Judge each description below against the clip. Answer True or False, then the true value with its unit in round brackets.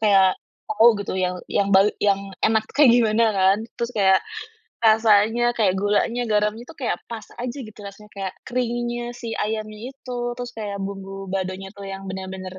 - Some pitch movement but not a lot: True (3.3 semitones)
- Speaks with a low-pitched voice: False (210 Hz)